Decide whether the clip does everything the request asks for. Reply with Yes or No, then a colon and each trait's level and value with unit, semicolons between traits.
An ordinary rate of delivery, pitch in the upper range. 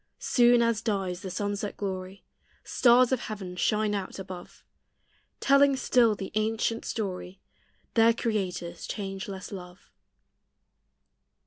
No: slow, 110 wpm; high, 205 Hz